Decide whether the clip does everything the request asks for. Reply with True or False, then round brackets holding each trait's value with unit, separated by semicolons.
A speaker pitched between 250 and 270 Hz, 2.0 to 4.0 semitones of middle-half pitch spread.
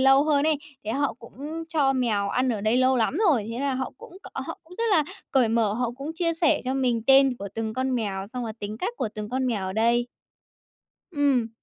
True (255 Hz; 3.5 semitones)